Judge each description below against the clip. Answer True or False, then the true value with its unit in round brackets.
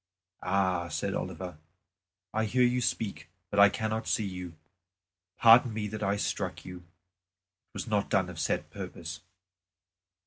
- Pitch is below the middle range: True (100 Hz)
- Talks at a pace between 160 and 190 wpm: False (145 wpm)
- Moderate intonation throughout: True (3.4 semitones)